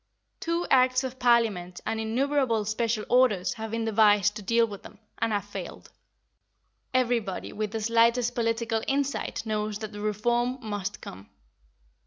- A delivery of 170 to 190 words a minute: No, average, 150 wpm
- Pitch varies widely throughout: No, narrow, 2.5 semitones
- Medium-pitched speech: No, high, 225 Hz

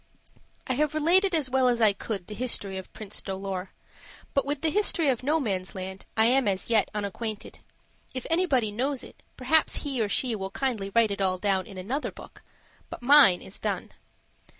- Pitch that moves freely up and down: Yes, wide, 5.9 semitones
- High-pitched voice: Yes, high, 230 Hz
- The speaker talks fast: No, average, 185 wpm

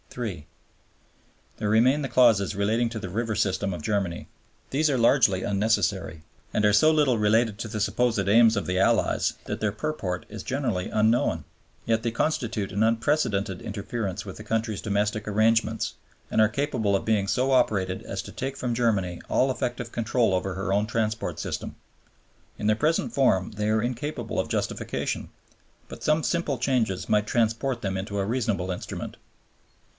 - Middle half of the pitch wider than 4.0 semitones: No, average, 3.4 semitones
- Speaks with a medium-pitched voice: No, low, 110 Hz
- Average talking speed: Yes, average, 170 wpm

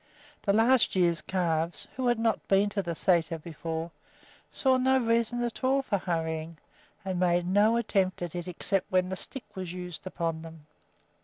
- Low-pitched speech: No, medium, 185 Hz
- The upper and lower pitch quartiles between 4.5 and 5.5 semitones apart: Yes, average, 5.0 semitones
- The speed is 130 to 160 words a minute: No, average, 175 wpm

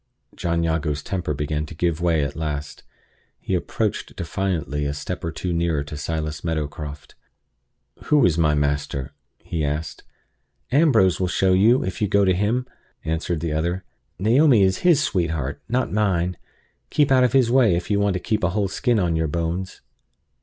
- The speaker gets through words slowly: No, average, 175 wpm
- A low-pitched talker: Yes, very low, 85 Hz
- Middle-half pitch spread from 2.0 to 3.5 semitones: No, average, 4.6 semitones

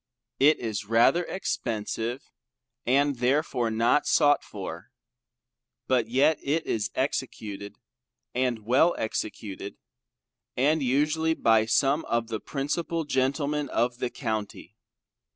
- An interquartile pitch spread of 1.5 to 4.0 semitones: No, average, 4.6 semitones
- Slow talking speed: Yes, slow, 110 wpm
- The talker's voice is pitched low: Yes, low, 125 Hz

